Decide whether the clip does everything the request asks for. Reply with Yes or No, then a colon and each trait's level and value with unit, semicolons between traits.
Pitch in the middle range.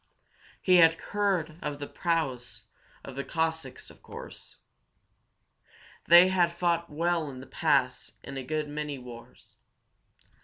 Yes: medium, 155 Hz